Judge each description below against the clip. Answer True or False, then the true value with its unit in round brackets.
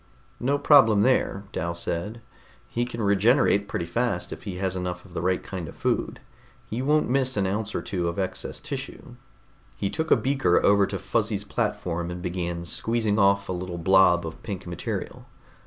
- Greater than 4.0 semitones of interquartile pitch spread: True (4.4 semitones)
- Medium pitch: False (100 Hz)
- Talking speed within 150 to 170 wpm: False (185 wpm)